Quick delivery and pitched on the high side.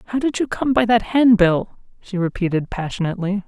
No: average, 175 wpm; high, 205 Hz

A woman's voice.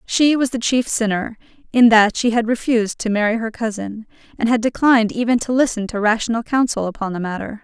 Yes: female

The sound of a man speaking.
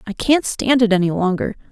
No: female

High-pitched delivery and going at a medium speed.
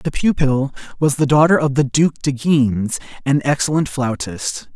No: medium, 140 Hz; average, 165 wpm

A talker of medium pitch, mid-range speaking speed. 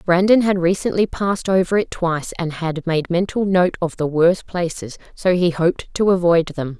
Yes: medium, 175 Hz; average, 195 wpm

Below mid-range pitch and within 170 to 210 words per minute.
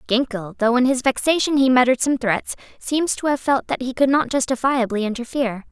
No: very high, 255 Hz; average, 200 wpm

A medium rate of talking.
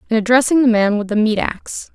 No: fast, 245 wpm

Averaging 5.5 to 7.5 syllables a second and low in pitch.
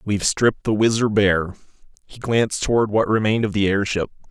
Yes: 6.0 syllables/s; low, 105 Hz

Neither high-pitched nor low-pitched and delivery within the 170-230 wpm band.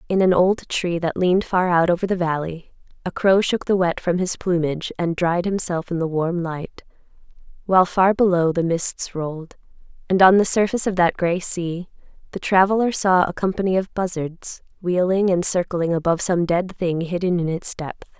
Yes: medium, 180 Hz; average, 190 wpm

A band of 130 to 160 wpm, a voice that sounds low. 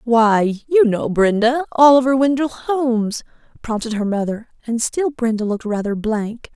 No: average, 145 wpm; high, 235 Hz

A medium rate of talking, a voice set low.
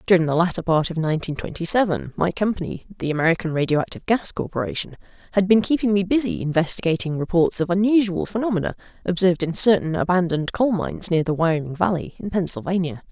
No: average, 170 wpm; medium, 180 Hz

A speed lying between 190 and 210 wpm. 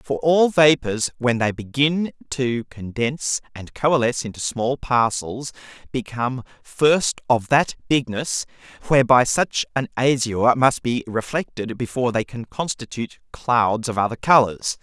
No: slow, 135 wpm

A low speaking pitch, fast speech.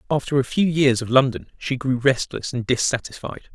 No: low, 130 Hz; average, 185 wpm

